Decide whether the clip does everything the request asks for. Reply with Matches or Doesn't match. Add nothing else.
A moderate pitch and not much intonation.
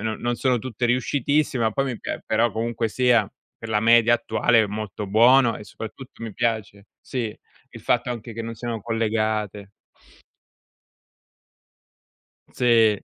Doesn't match